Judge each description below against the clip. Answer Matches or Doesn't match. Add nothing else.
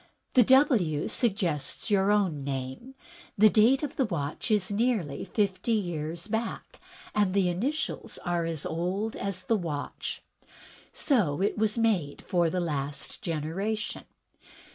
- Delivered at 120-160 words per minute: Matches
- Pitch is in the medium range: Doesn't match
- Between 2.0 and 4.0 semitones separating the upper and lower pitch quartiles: Doesn't match